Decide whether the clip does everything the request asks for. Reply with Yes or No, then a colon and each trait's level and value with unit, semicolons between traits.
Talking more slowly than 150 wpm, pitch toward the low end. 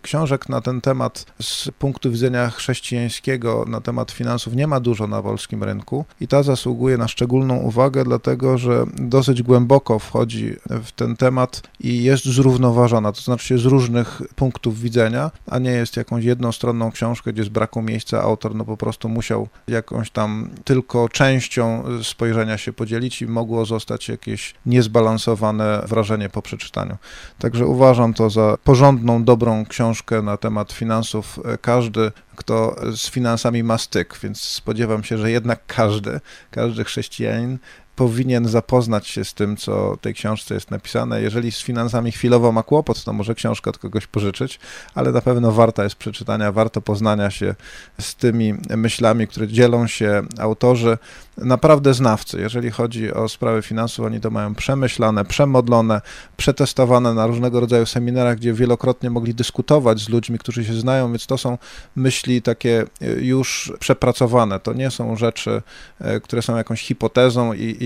No: average, 155 wpm; low, 115 Hz